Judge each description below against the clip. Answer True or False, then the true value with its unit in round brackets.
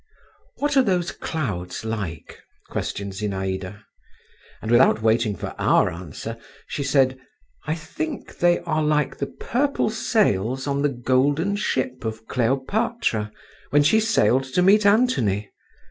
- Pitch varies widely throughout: True (8.6 semitones)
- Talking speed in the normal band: False (130 wpm)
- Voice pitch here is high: False (130 Hz)